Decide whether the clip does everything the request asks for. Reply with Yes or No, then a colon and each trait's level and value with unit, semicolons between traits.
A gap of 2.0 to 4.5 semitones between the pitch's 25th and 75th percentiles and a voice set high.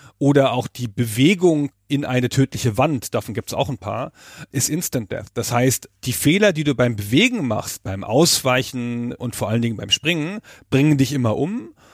No: average, 3.1 semitones; low, 130 Hz